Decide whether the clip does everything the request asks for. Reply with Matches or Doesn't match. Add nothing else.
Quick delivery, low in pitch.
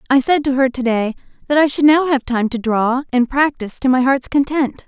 Doesn't match